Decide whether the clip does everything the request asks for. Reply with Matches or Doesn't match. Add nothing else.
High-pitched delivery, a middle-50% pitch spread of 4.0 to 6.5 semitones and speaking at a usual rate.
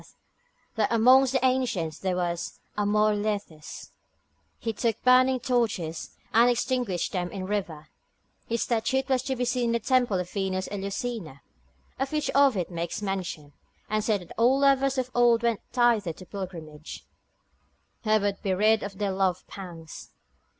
Matches